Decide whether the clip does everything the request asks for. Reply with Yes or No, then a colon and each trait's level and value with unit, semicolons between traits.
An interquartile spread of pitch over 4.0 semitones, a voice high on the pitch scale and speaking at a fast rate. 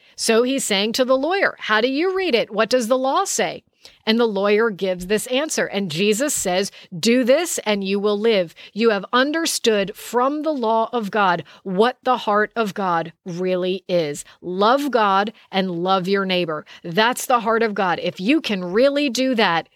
No: average, 4.7 semitones; high, 215 Hz; average, 190 wpm